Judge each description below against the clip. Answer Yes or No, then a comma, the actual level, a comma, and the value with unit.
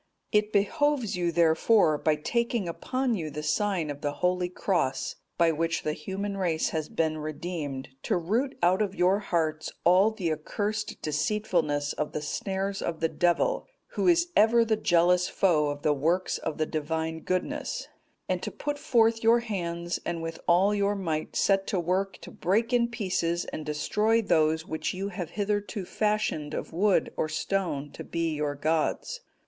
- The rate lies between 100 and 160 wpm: No, average, 175 wpm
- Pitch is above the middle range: No, medium, 180 Hz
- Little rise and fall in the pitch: No, average, 4.8 semitones